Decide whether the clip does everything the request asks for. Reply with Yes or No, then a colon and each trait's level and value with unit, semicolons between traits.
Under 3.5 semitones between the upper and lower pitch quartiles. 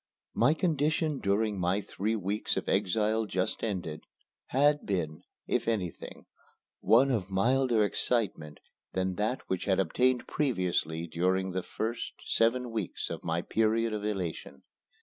No: average, 4.2 semitones